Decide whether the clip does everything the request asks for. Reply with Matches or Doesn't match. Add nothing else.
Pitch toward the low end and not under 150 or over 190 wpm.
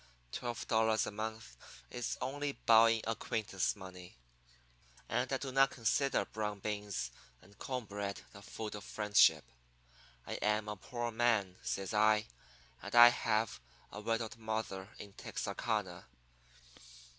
Doesn't match